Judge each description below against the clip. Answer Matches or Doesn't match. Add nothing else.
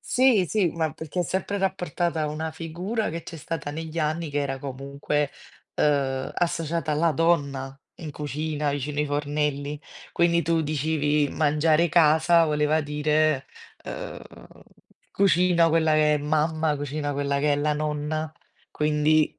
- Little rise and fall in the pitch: Matches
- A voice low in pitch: Doesn't match